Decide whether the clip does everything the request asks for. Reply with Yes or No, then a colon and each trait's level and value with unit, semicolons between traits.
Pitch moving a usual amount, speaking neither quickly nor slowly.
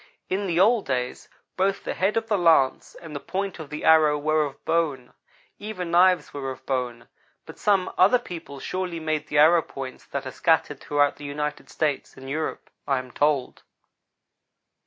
Yes: average, 4.6 semitones; average, 180 wpm